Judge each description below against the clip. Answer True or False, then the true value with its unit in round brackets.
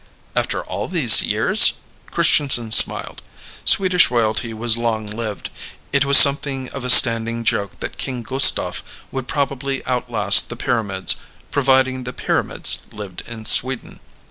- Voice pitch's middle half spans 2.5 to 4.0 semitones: True (3.1 semitones)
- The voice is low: True (120 Hz)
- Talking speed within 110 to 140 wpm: True (135 wpm)